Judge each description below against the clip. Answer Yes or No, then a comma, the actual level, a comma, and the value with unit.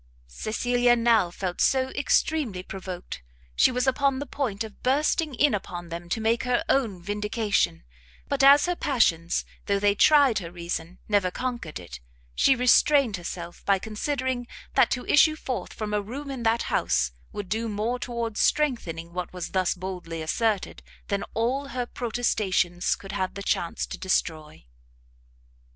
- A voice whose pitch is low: No, high, 220 Hz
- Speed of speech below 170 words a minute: Yes, average, 155 wpm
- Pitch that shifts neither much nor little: No, wide, 5.8 semitones